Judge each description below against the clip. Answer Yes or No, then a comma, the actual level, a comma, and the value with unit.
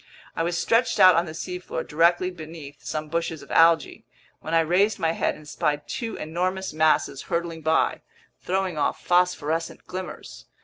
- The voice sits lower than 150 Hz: No, medium, 165 Hz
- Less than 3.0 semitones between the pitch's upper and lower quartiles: Yes, narrow, 2.4 semitones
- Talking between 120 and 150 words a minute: No, average, 165 wpm